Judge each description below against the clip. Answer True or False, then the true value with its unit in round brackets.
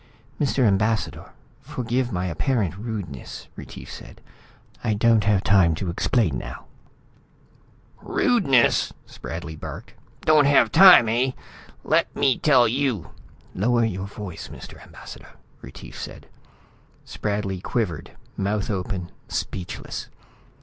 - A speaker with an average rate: False (115 wpm)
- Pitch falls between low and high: False (105 Hz)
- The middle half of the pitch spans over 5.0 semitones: False (4.7 semitones)